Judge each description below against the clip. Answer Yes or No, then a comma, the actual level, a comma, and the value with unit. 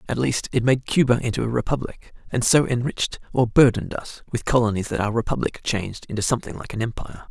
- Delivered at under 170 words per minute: No, fast, 205 wpm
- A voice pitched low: Yes, low, 120 Hz